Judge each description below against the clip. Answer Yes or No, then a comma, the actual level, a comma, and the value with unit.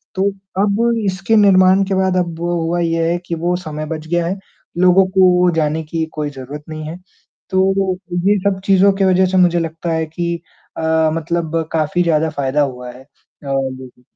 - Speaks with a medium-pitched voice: Yes, medium, 170 Hz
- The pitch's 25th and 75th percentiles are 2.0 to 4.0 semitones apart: Yes, average, 3.1 semitones